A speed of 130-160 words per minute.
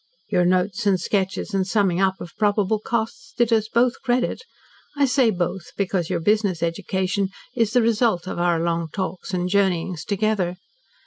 No: average, 170 wpm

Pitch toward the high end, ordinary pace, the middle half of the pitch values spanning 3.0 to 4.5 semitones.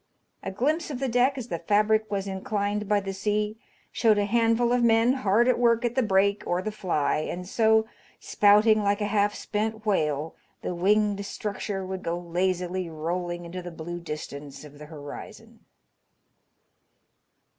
Yes: high, 205 Hz; average, 165 wpm; average, 3.8 semitones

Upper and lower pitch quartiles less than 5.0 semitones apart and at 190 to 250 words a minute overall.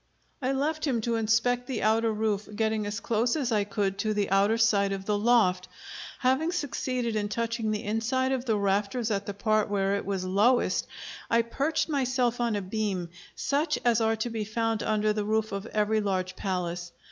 Yes: average, 2.8 semitones; average, 195 wpm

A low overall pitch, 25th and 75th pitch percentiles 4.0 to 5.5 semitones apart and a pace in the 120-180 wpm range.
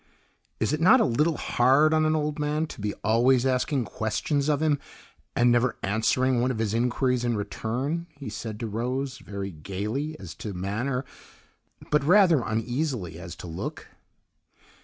Yes: low, 125 Hz; average, 5.2 semitones; average, 165 wpm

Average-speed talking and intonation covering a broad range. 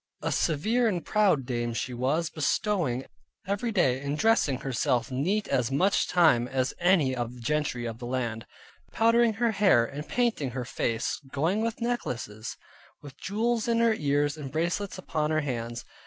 Yes: average, 170 wpm; wide, 8.4 semitones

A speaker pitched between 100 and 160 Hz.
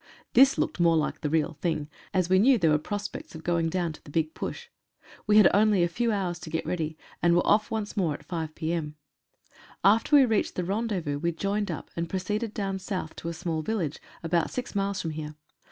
No: medium, 175 Hz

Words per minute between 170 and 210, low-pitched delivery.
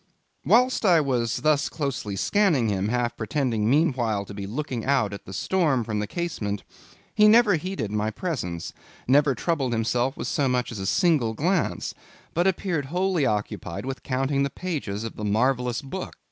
Yes: average, 175 wpm; low, 130 Hz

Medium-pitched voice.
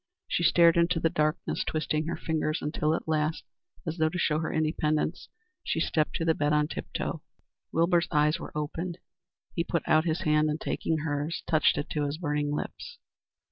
Yes: medium, 155 Hz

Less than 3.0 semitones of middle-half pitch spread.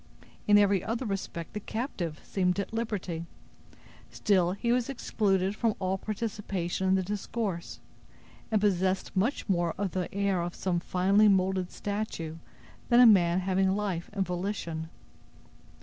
Yes: narrow, 2.6 semitones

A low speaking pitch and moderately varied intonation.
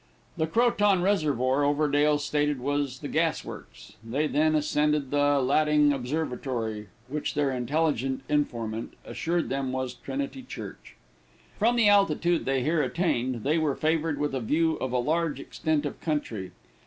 No: medium, 145 Hz; average, 3.3 semitones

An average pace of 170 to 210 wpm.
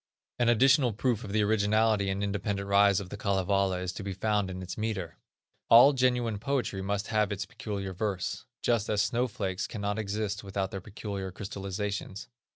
Yes: average, 175 wpm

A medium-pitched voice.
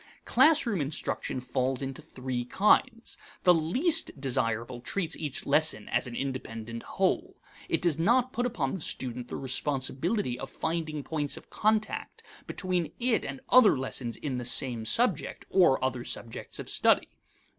Yes: medium, 145 Hz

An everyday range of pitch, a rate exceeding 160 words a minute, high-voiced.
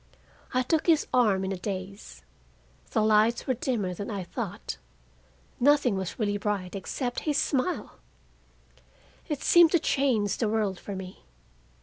No: average, 5.0 semitones; average, 145 wpm; high, 215 Hz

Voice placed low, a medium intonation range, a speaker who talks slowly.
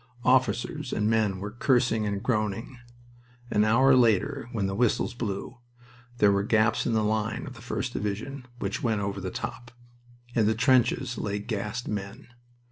No: low, 110 Hz; average, 3.0 semitones; average, 165 wpm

